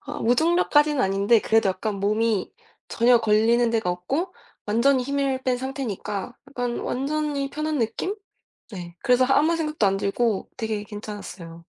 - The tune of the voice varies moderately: Yes, average, 5.0 semitones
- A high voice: Yes, high, 235 Hz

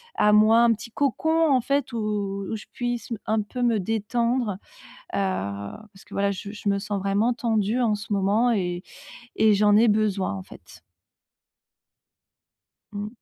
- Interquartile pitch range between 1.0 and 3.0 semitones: Yes, average, 2.7 semitones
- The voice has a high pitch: Yes, high, 215 Hz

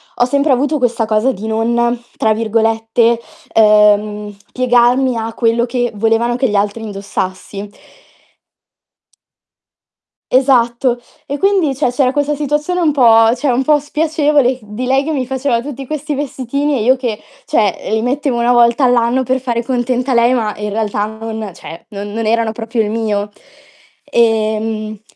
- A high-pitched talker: Yes, high, 235 Hz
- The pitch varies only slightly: No, average, 3.1 semitones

